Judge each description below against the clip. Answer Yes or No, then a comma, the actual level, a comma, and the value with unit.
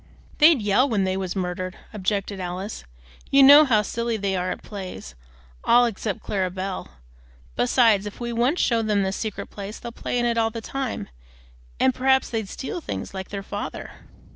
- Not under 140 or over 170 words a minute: No, average, 185 wpm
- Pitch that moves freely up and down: No, average, 3.8 semitones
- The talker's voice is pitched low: No, high, 210 Hz